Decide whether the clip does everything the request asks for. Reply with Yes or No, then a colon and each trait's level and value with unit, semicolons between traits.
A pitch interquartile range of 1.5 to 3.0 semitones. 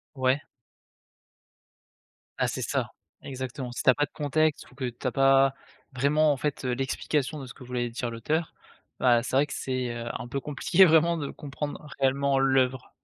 Yes: narrow, 2.5 semitones